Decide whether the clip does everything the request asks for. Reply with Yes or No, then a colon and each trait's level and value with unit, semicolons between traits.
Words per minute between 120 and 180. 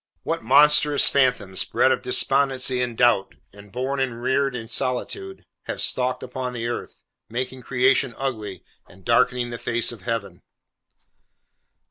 Yes: average, 140 wpm